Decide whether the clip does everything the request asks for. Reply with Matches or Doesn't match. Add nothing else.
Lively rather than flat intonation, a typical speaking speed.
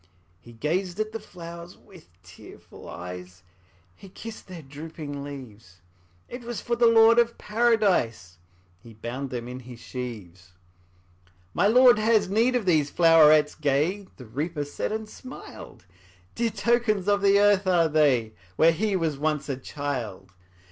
Matches